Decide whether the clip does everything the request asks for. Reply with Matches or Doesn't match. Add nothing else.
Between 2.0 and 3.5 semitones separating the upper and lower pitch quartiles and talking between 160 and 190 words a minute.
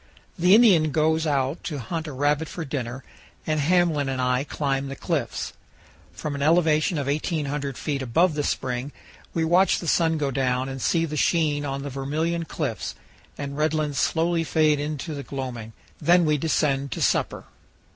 Matches